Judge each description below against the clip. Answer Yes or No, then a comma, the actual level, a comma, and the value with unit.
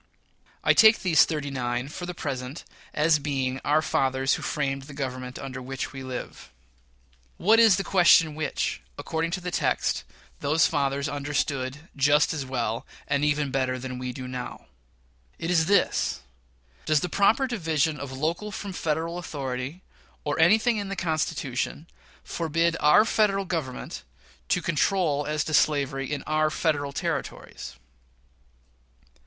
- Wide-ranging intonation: No, average, 3.8 semitones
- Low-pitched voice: No, medium, 150 Hz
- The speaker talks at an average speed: Yes, average, 150 wpm